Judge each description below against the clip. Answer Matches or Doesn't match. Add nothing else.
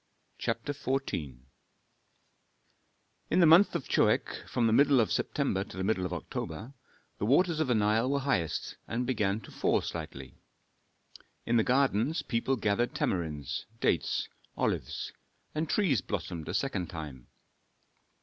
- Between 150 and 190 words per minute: Doesn't match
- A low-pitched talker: Matches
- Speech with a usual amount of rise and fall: Doesn't match